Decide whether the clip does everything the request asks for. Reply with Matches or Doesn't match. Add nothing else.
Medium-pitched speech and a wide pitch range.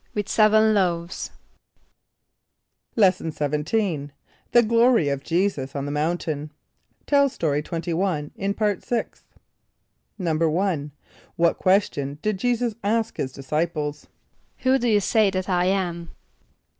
Matches